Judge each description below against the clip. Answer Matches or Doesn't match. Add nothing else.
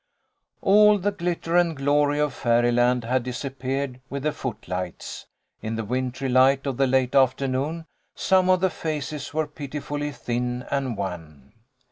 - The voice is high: Doesn't match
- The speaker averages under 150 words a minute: Doesn't match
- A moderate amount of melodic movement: Matches